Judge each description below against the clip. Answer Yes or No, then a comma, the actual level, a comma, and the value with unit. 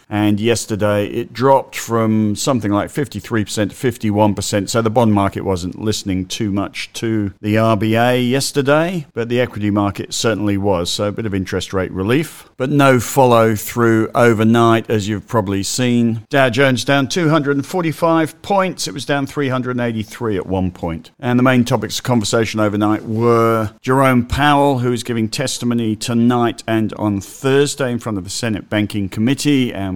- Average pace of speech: Yes, average, 165 wpm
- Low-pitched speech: Yes, low, 115 Hz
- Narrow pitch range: No, average, 3.6 semitones